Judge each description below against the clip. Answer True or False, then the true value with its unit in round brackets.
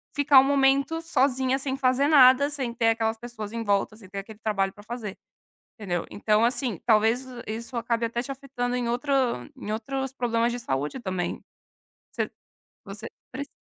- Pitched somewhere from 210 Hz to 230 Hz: False (240 Hz)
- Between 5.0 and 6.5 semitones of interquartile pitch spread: False (3.6 semitones)